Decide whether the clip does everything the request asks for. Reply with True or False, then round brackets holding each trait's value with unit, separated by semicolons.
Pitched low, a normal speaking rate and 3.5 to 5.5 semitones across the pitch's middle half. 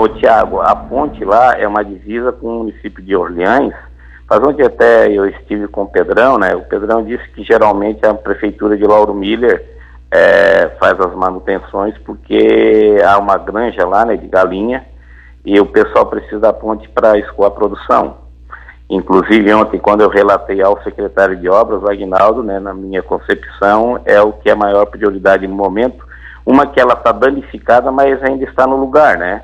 False (105 Hz; 175 wpm; 2.6 semitones)